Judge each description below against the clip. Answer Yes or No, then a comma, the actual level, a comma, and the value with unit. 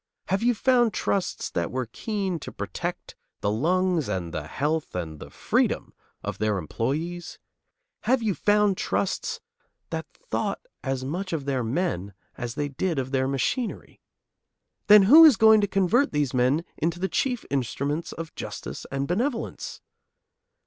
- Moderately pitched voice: Yes, medium, 165 Hz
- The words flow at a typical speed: Yes, average, 155 wpm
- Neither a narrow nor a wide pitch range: No, wide, 7.7 semitones